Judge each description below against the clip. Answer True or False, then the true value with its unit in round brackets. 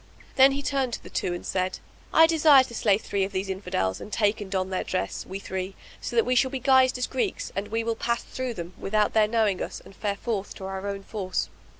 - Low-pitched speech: False (210 Hz)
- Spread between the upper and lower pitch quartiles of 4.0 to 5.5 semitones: True (4.6 semitones)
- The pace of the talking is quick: True (255 wpm)